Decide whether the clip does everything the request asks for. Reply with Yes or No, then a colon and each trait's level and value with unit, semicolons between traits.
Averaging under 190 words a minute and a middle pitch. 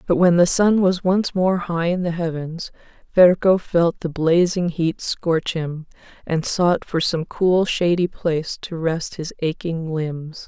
Yes: average, 170 wpm; medium, 170 Hz